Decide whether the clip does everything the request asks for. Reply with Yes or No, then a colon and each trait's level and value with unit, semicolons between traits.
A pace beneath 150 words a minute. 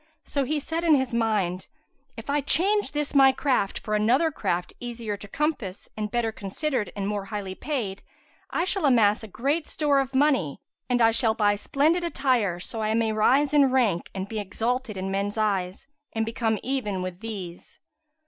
No: average, 180 wpm